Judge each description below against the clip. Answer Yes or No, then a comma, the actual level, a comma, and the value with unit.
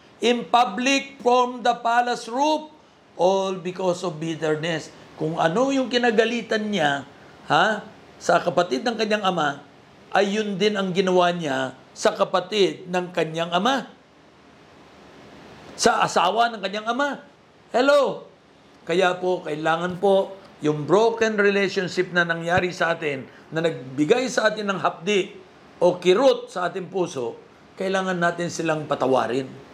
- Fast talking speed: No, average, 130 wpm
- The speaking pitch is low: No, high, 190 Hz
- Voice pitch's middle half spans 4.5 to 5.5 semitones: Yes, average, 5.2 semitones